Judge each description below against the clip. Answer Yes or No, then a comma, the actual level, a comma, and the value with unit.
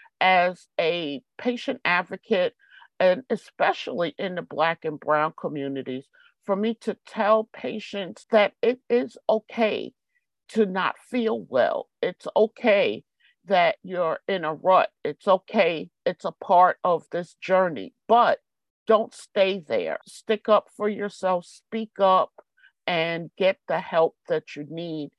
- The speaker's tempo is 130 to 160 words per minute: Yes, slow, 135 wpm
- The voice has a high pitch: Yes, high, 195 Hz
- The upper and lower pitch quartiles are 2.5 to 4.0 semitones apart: No, average, 5.1 semitones